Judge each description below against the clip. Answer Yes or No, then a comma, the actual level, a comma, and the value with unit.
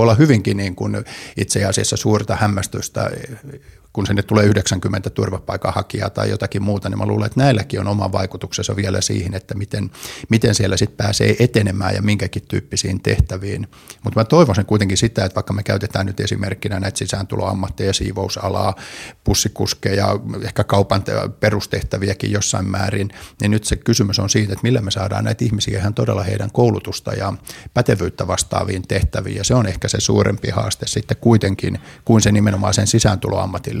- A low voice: Yes, low, 100 Hz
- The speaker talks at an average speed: No, fast, 160 wpm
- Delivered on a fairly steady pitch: Yes, narrow, 2.0 semitones